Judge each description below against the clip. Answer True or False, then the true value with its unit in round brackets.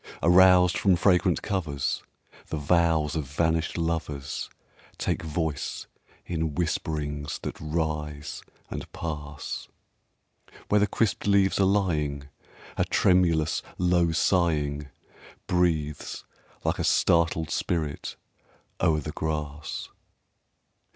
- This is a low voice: True (80 Hz)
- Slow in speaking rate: True (100 wpm)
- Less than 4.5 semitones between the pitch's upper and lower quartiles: True (2.9 semitones)